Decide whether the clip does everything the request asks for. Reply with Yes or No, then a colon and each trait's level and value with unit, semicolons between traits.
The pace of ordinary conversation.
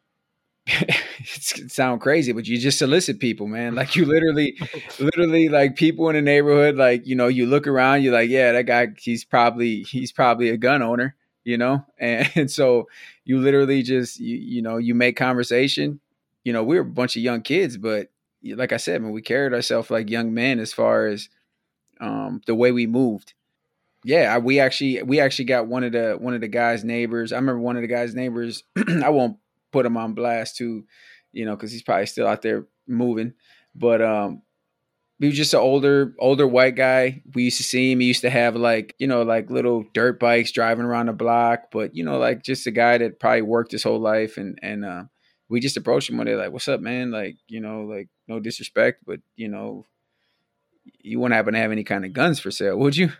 No: fast, 220 wpm